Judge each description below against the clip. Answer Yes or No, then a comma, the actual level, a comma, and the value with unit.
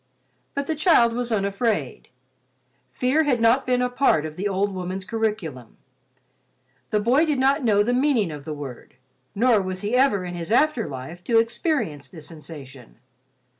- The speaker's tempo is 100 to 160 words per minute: No, average, 170 wpm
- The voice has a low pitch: No, high, 215 Hz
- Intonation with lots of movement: Yes, wide, 6.6 semitones